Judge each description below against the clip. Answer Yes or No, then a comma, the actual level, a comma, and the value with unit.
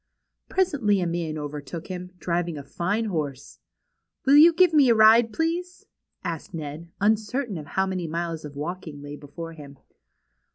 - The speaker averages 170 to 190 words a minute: No, average, 160 wpm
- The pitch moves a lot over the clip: Yes, wide, 6.2 semitones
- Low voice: No, medium, 175 Hz